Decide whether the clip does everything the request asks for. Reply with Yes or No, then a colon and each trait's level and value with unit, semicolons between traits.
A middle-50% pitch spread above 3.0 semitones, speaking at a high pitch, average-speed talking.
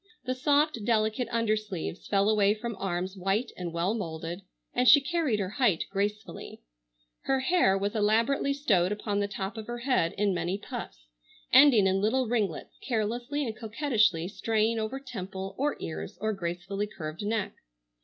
Yes: average, 3.9 semitones; high, 210 Hz; average, 160 wpm